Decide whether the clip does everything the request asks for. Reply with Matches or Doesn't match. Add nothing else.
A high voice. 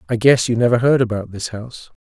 Doesn't match